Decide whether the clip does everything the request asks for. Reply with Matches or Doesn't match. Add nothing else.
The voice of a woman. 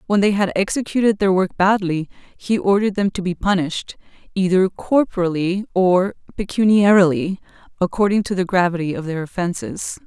Matches